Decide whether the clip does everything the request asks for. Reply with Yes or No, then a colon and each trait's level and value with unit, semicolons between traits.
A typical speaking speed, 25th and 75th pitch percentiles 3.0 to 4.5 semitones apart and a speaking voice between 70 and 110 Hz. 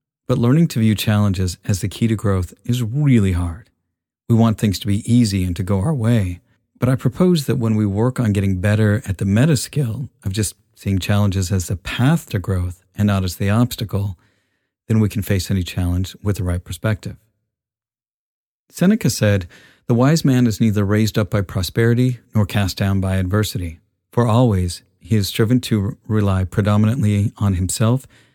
Yes: average, 185 wpm; average, 3.4 semitones; low, 105 Hz